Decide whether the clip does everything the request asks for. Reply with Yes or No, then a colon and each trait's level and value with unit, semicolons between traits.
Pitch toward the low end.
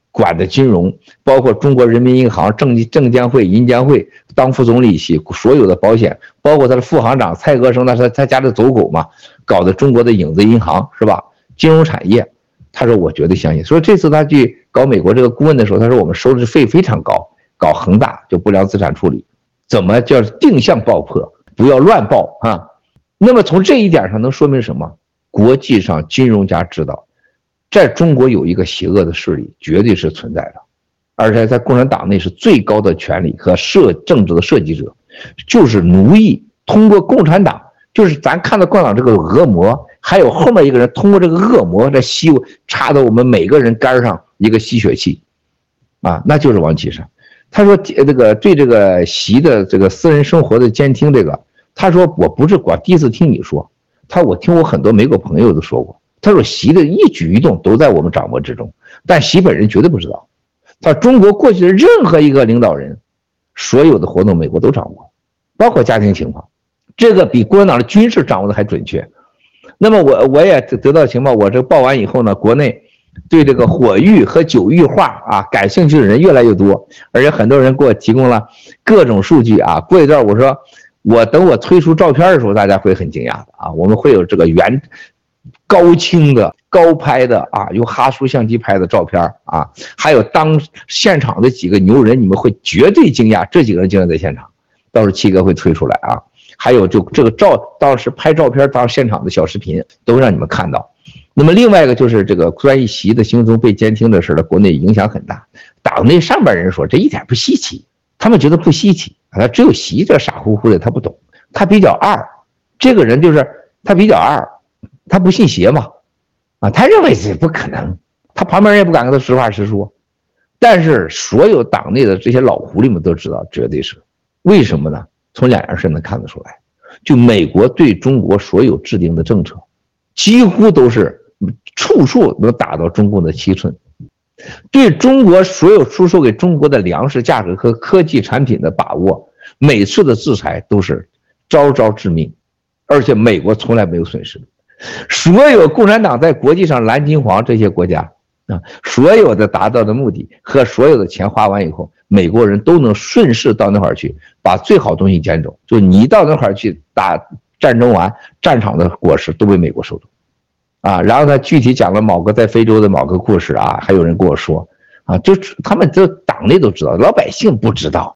Yes: low, 125 Hz